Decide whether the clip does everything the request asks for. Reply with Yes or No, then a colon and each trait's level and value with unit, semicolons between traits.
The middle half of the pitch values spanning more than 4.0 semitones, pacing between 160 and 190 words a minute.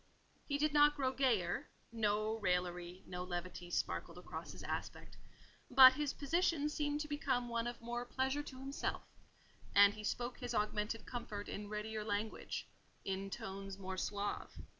No: average, 5.0 semitones; average, 145 wpm